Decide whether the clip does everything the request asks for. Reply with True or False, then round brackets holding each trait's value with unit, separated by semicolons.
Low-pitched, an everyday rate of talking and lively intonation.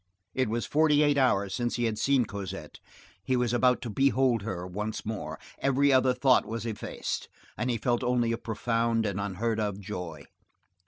False (115 Hz; 180 wpm; 3.7 semitones)